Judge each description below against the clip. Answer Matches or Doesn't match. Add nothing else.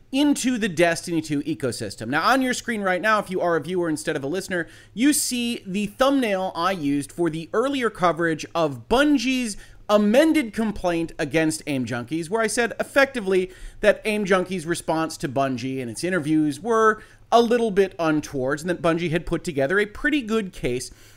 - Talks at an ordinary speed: Matches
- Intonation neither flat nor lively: Doesn't match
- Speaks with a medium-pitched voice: Matches